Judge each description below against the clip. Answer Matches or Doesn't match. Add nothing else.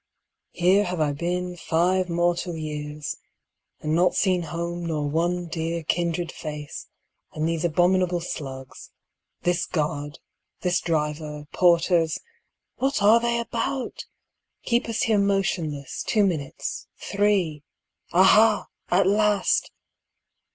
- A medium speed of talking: Doesn't match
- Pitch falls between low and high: Matches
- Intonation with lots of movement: Doesn't match